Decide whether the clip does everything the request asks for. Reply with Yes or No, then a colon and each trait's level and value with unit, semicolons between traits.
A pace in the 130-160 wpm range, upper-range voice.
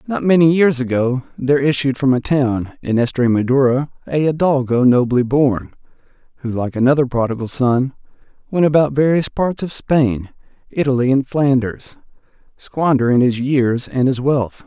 No: average, 145 wpm; low, 135 Hz